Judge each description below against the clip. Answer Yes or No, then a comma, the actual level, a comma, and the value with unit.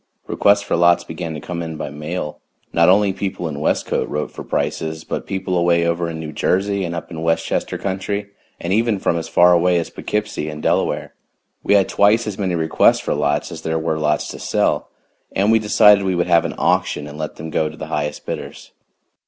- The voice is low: Yes, very low, 85 Hz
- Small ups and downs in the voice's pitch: No, average, 3.5 semitones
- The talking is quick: Yes, fast, 215 wpm